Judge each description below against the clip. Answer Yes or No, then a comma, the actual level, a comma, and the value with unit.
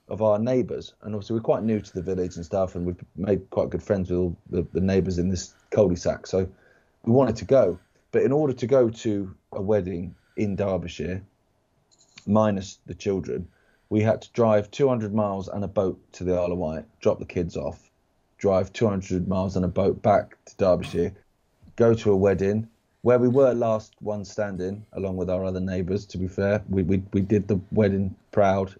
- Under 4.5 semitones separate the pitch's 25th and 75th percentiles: Yes, narrow, 2.6 semitones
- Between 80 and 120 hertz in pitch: Yes, low, 100 Hz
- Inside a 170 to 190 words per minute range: No, average, 200 wpm